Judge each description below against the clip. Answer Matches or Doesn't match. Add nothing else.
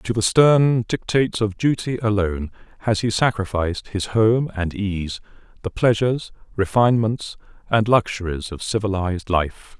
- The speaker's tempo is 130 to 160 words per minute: Matches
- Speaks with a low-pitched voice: Matches